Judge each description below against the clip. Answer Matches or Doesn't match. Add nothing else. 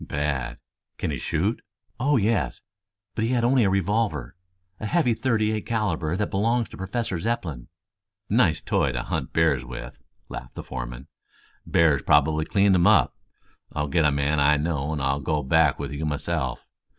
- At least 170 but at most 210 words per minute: Matches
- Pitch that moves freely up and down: Matches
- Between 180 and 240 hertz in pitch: Doesn't match